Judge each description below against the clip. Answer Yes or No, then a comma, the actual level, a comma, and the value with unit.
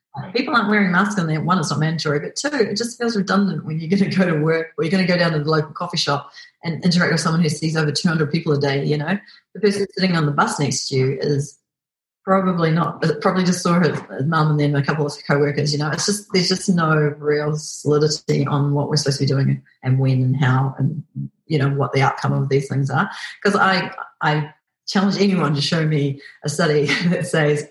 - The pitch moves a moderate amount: Yes, average, 4.1 semitones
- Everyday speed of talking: No, fast, 245 wpm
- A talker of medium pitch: Yes, medium, 155 Hz